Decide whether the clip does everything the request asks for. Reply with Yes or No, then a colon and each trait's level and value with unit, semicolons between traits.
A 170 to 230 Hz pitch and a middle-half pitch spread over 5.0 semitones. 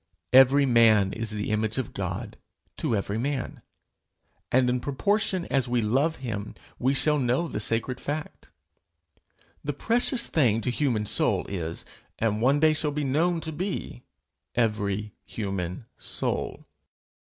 No: low, 125 Hz; wide, 5.4 semitones